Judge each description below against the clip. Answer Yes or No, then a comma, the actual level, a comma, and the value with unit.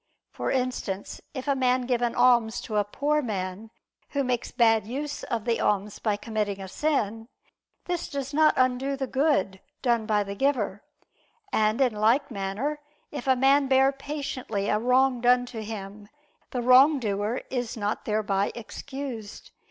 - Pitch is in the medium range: No, high, 245 Hz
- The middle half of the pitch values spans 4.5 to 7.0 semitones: No, average, 4.1 semitones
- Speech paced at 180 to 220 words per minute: No, average, 160 wpm